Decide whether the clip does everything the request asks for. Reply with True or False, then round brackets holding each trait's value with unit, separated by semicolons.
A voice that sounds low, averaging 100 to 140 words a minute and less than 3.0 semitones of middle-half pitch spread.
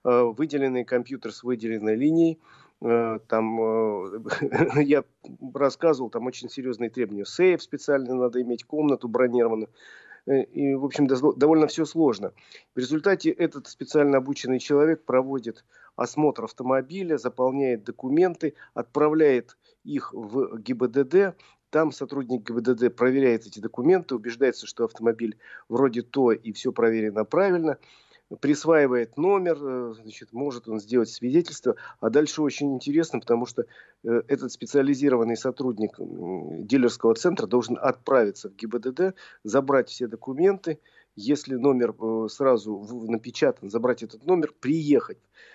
False (130 Hz; 115 wpm; 4.0 semitones)